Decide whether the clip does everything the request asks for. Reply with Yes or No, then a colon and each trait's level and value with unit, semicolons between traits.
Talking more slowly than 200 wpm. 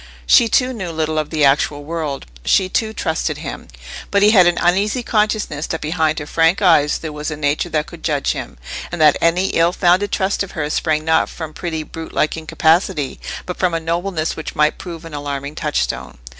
No: fast, 205 wpm